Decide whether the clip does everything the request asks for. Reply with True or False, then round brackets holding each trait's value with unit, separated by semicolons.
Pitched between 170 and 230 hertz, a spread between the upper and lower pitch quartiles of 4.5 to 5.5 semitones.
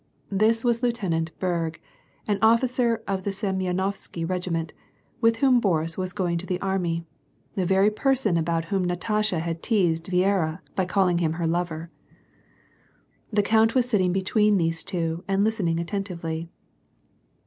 False (185 Hz; 4.0 semitones)